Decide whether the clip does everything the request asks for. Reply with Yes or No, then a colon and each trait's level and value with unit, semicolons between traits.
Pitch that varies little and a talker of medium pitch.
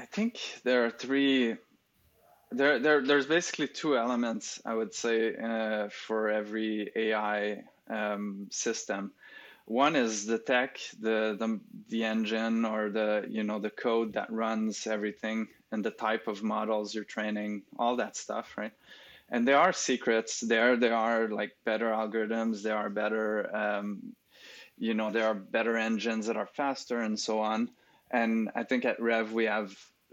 No: narrow, 1.3 semitones; low, 110 Hz